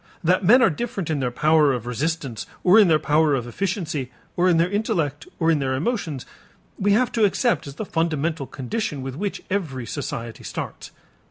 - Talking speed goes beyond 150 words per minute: Yes, average, 190 wpm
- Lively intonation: Yes, wide, 5.7 semitones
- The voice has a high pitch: No, medium, 160 Hz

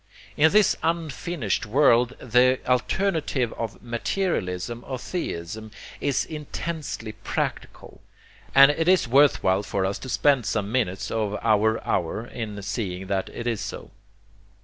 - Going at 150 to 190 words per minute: No, slow, 135 wpm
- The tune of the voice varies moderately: No, wide, 5.7 semitones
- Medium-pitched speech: No, low, 120 Hz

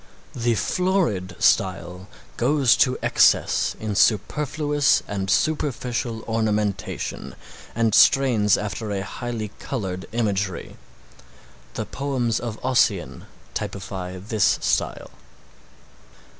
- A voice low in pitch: Yes, low, 110 Hz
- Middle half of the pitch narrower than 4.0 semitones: No, average, 4.3 semitones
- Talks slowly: Yes, slow, 90 wpm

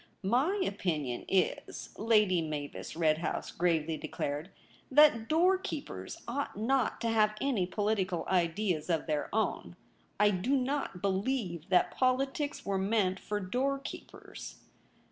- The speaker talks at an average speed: No, slow, 125 wpm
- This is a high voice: Yes, high, 205 Hz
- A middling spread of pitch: No, wide, 6.6 semitones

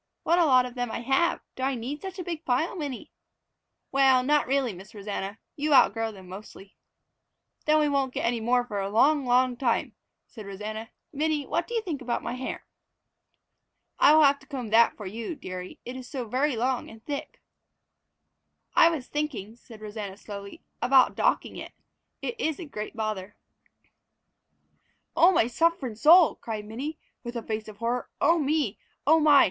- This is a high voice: Yes, very high, 250 Hz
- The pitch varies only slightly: No, average, 5.1 semitones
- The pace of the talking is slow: No, average, 185 wpm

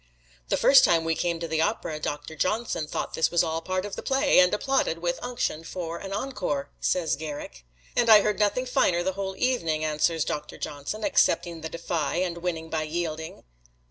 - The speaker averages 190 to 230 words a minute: Yes, average, 200 wpm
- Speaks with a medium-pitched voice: Yes, medium, 170 Hz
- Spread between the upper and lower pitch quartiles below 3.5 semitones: No, average, 3.8 semitones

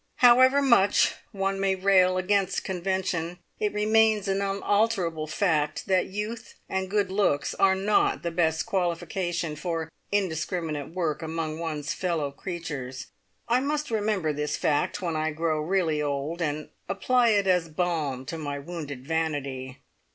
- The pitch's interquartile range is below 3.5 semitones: No, average, 4.0 semitones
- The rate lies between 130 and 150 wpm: Yes, average, 145 wpm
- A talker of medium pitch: Yes, medium, 175 Hz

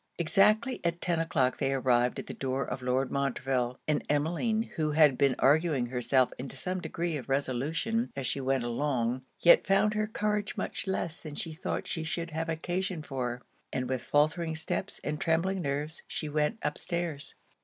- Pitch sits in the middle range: Yes, medium, 150 Hz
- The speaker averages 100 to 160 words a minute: No, average, 180 wpm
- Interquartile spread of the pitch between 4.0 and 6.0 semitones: Yes, average, 4.5 semitones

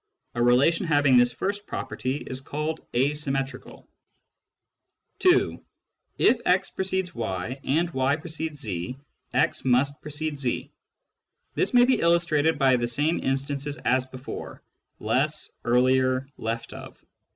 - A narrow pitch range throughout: No, average, 3.8 semitones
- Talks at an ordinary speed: No, slow, 125 wpm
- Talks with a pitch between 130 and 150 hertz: Yes, medium, 140 Hz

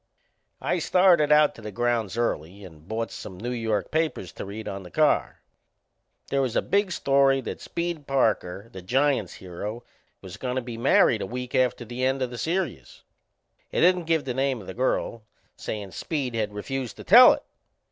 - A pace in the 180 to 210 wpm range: Yes, average, 190 wpm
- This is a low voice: Yes, low, 120 Hz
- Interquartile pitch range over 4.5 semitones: Yes, average, 5.1 semitones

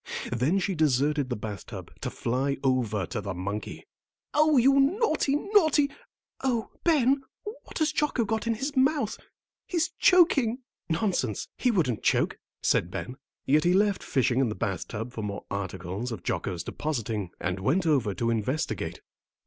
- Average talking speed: Yes, average, 160 wpm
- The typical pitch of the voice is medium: Yes, medium, 150 Hz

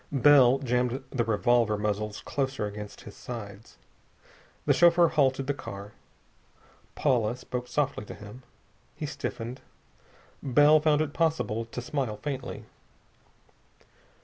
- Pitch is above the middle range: No, low, 125 Hz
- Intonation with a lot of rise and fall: No, average, 4.9 semitones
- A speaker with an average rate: No, slow, 120 wpm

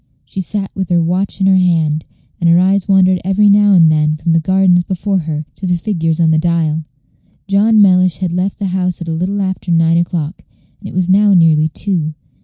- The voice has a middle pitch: Yes, medium, 180 Hz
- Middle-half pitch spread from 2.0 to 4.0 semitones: Yes, average, 2.8 semitones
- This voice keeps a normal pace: No, fast, 215 wpm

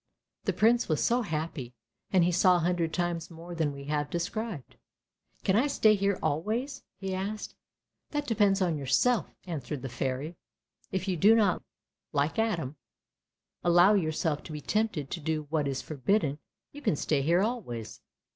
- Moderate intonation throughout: No, wide, 5.7 semitones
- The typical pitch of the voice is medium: Yes, medium, 175 Hz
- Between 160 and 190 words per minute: Yes, average, 180 wpm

